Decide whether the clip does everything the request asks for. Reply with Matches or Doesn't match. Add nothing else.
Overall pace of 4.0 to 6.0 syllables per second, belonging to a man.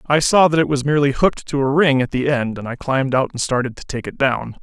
Doesn't match